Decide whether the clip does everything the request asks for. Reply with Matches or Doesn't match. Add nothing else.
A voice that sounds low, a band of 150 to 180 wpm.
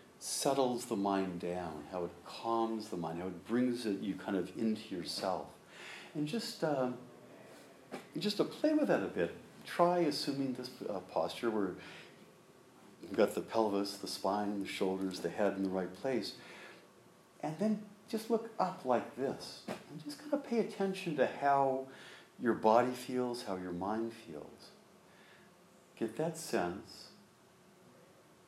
Matches